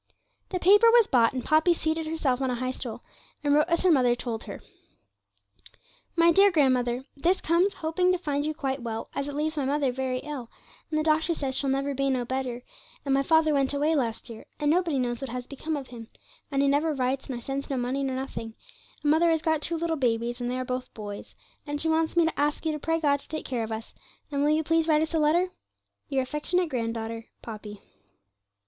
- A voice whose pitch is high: Yes, very high, 280 Hz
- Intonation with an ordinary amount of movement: Yes, average, 4.0 semitones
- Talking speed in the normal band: No, fast, 230 wpm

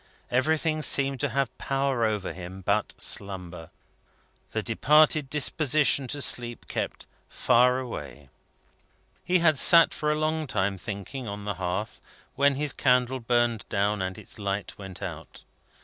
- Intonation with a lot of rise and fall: Yes, wide, 6.1 semitones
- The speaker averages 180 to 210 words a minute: No, average, 145 wpm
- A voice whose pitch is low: Yes, low, 120 Hz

